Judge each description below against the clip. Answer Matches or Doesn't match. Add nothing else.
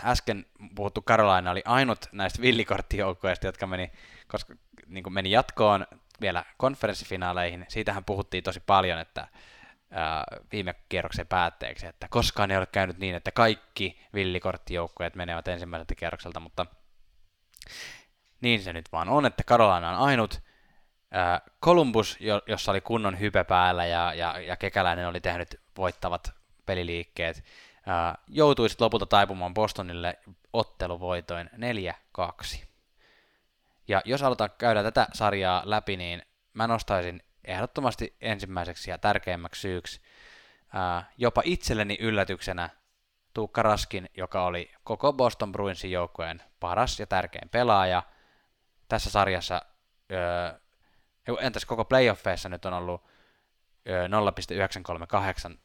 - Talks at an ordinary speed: Matches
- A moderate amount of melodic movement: Matches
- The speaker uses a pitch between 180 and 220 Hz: Doesn't match